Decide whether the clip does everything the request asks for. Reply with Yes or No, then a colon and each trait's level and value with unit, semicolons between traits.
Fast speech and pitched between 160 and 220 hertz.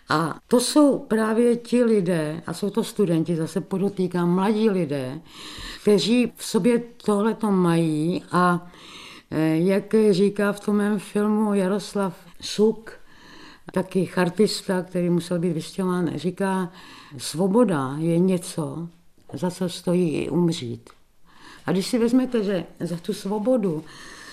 No: average, 125 wpm; high, 190 Hz